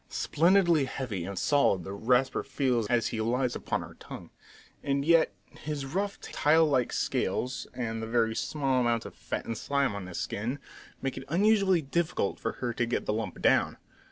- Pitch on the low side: Yes, low, 130 Hz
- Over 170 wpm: Yes, average, 185 wpm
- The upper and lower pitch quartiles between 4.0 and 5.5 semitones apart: Yes, average, 4.8 semitones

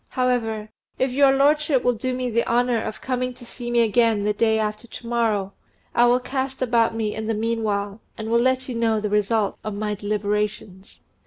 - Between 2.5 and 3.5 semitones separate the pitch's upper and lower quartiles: Yes, average, 2.9 semitones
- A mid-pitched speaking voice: No, high, 230 Hz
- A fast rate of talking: Yes, fast, 210 wpm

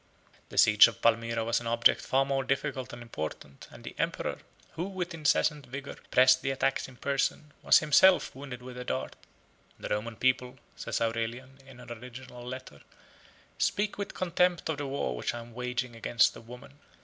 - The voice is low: Yes, low, 130 Hz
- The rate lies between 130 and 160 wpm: No, average, 185 wpm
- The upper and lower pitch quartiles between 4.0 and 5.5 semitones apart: No, average, 3.0 semitones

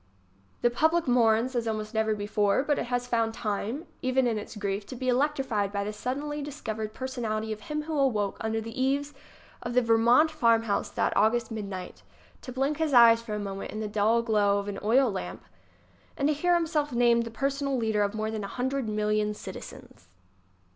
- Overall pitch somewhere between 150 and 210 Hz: No, high, 230 Hz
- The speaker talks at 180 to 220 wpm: Yes, average, 195 wpm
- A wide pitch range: No, average, 3.9 semitones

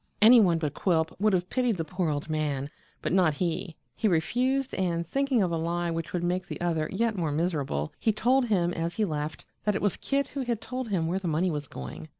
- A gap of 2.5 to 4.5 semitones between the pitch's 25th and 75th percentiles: No, average, 5.0 semitones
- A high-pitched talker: No, medium, 175 Hz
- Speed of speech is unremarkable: No, fast, 235 wpm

